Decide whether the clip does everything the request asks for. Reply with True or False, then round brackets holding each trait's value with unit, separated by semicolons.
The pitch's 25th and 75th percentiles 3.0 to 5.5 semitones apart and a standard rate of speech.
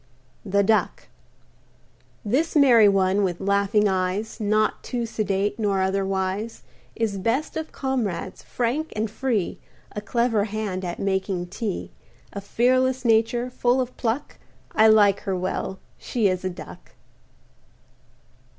False (3.5 semitones; 130 wpm)